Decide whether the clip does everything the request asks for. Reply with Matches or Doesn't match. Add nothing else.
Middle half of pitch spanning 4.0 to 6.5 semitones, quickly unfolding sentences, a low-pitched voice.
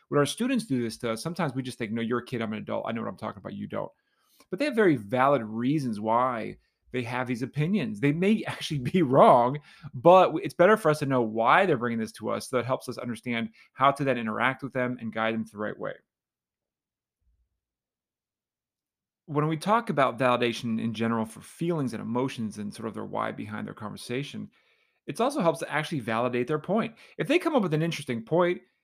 Matches